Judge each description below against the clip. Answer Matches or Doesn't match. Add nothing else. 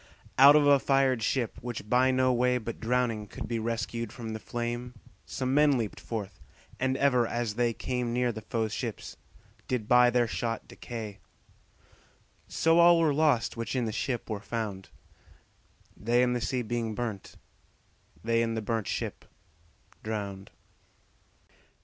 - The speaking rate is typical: Matches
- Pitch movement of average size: Doesn't match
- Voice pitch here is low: Matches